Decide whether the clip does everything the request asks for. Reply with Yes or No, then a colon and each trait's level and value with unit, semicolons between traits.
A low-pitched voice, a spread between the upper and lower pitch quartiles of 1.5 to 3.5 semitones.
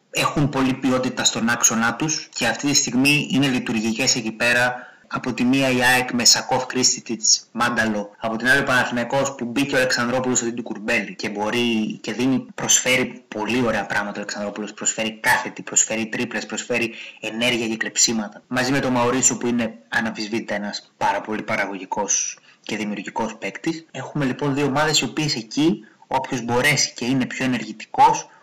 Yes: low, 125 Hz; average, 2.7 semitones